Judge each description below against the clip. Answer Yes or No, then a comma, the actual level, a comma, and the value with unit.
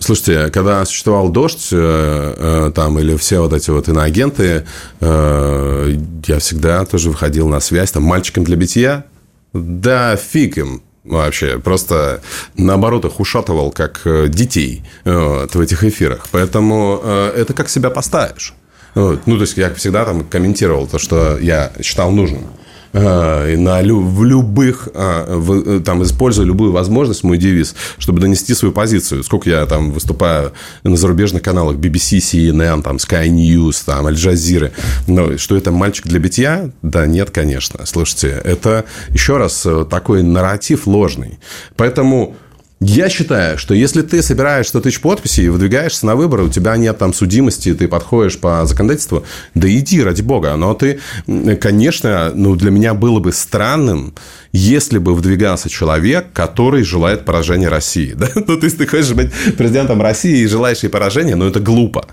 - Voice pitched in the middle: No, very low, 90 Hz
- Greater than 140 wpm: Yes, average, 155 wpm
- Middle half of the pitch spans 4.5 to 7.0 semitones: Yes, average, 4.8 semitones